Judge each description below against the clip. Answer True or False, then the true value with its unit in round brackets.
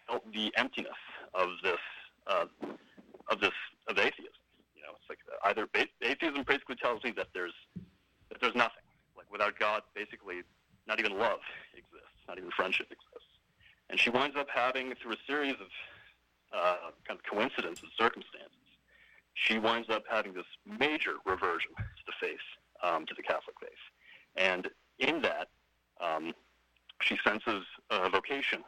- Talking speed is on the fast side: False (155 wpm)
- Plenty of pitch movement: True (8.2 semitones)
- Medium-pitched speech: False (110 Hz)